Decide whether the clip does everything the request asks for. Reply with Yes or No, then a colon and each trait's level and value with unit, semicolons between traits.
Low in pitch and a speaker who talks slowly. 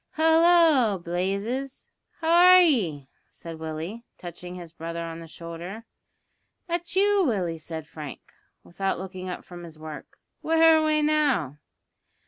No: high, 190 Hz; slow, 130 wpm